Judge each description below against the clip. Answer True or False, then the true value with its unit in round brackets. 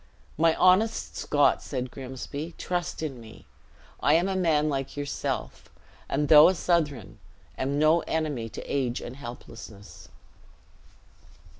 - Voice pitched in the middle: True (145 Hz)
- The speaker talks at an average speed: False (130 wpm)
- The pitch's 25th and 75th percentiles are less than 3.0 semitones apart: False (4.0 semitones)